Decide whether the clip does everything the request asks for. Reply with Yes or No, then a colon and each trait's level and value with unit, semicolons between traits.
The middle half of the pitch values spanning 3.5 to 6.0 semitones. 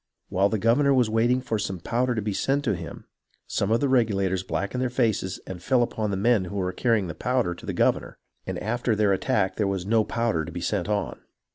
Yes: average, 4.0 semitones